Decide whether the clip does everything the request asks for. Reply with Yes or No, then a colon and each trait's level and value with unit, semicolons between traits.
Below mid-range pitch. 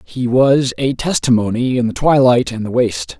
Yes: low, 125 Hz